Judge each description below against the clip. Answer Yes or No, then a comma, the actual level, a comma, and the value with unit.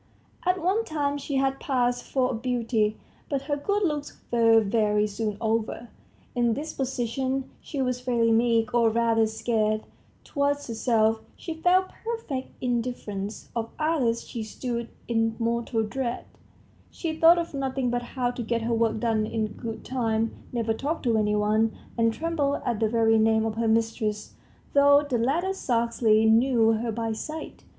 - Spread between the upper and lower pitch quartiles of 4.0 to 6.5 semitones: No, average, 3.4 semitones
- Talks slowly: No, average, 160 wpm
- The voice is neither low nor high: No, high, 235 Hz